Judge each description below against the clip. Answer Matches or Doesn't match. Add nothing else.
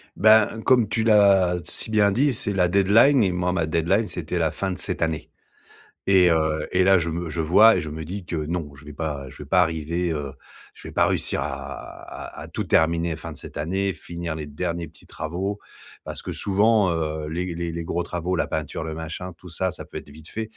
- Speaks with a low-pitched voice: Matches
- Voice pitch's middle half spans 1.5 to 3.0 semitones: Doesn't match